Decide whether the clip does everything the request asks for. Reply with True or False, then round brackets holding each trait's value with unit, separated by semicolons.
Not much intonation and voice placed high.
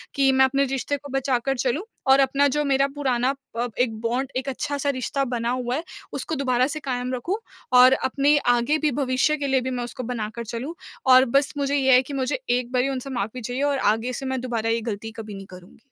True (2.2 semitones; 260 Hz)